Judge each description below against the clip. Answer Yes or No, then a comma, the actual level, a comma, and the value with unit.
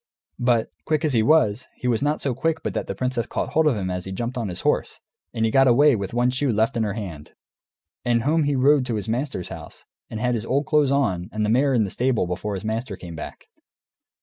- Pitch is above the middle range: No, low, 120 Hz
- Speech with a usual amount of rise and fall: Yes, average, 4.4 semitones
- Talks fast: Yes, fast, 255 wpm